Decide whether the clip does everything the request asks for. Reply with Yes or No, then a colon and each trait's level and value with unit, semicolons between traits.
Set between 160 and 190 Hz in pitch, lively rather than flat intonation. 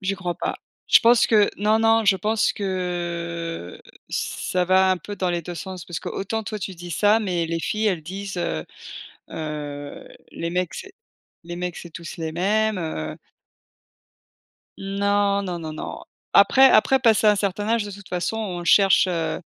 No: medium, 185 Hz; average, 3.3 semitones